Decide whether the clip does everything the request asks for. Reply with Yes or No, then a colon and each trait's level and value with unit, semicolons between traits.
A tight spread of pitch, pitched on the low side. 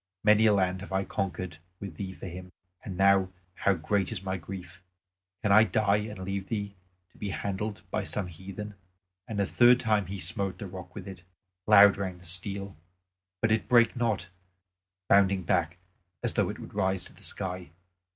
Yes: narrow, 2.1 semitones; low, 100 Hz